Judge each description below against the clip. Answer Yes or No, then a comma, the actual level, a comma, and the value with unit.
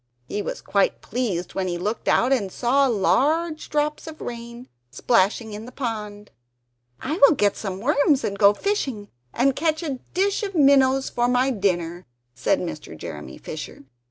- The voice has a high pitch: Yes, high, 240 Hz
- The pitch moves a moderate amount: No, wide, 5.9 semitones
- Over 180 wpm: No, average, 165 wpm